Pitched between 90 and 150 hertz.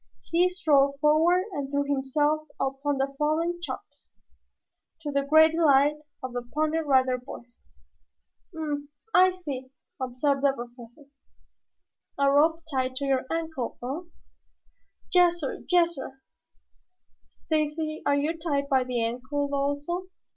No: very high, 285 Hz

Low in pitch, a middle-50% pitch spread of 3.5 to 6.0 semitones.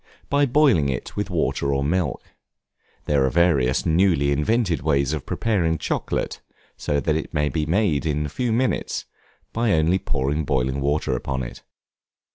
Yes: very low, 75 Hz; average, 4.7 semitones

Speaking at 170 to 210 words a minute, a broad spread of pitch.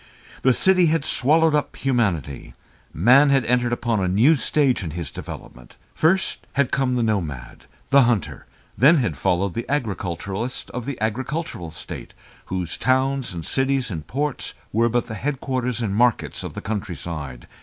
No: average, 160 wpm; wide, 6.2 semitones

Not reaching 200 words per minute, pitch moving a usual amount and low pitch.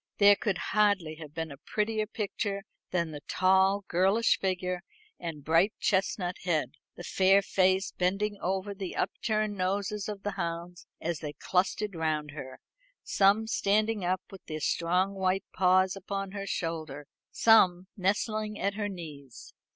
No: average, 150 wpm; average, 3.0 semitones; high, 190 Hz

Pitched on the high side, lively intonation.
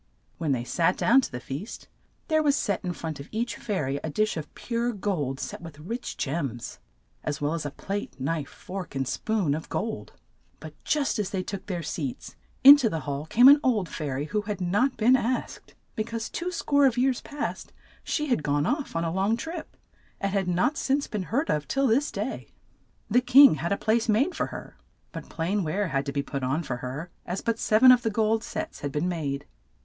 Yes: high, 195 Hz; wide, 7.9 semitones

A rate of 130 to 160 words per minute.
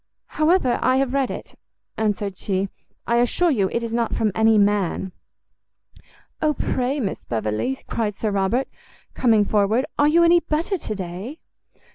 Yes: average, 155 wpm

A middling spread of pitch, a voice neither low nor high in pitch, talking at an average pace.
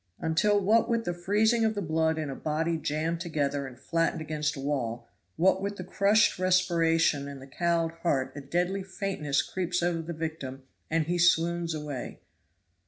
Yes: average, 3.6 semitones; medium, 165 Hz; average, 175 wpm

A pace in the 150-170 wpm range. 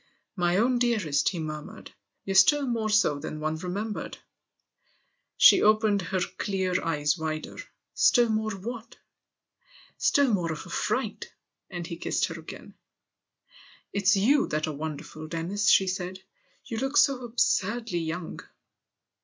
Yes: average, 160 wpm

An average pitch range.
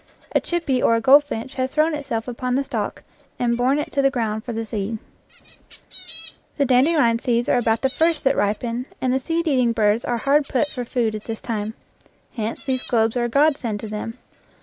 Yes: average, 3.4 semitones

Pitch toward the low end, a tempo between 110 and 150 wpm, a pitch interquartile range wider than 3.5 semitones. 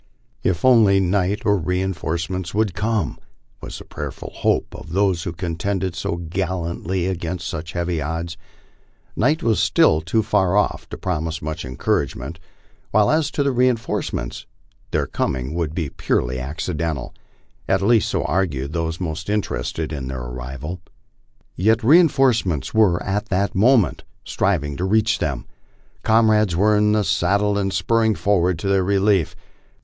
Yes: very low, 90 Hz; average, 145 wpm; average, 4.1 semitones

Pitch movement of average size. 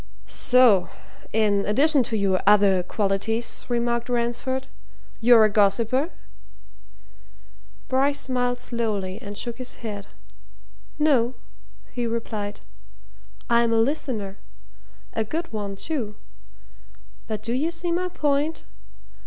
Yes: average, 3.9 semitones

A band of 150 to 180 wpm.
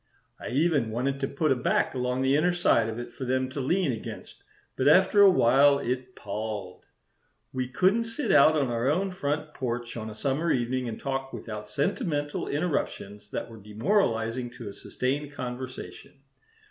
Yes: average, 175 wpm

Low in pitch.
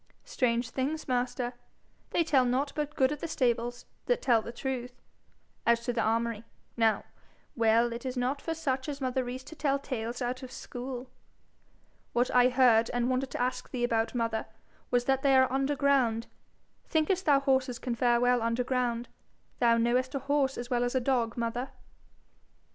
No: very high, 250 Hz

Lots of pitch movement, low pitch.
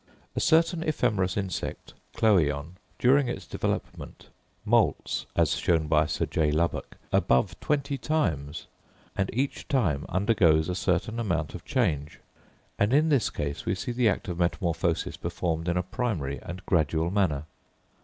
Yes: wide, 7.1 semitones; very low, 90 Hz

